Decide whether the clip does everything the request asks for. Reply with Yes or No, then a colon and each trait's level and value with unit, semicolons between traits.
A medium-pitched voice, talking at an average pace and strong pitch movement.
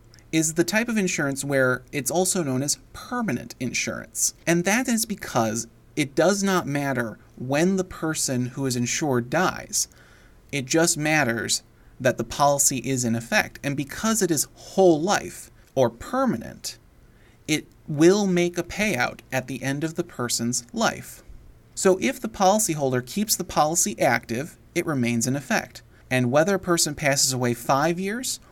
Yes: medium, 145 Hz; average, 160 wpm; wide, 6.5 semitones